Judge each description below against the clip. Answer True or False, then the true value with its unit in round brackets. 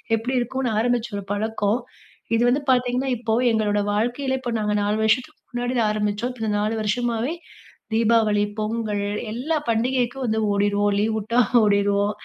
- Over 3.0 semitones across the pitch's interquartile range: False (2.7 semitones)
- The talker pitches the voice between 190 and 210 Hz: False (225 Hz)